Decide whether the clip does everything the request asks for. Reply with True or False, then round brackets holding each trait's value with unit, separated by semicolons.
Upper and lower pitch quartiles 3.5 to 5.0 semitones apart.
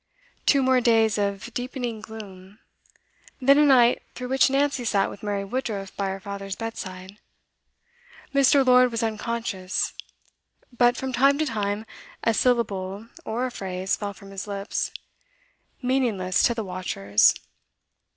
True (4.2 semitones)